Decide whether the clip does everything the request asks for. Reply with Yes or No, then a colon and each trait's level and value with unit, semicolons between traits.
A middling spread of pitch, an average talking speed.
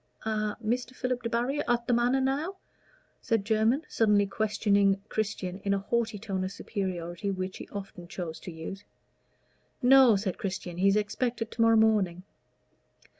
Yes: average, 3.4 semitones; average, 155 wpm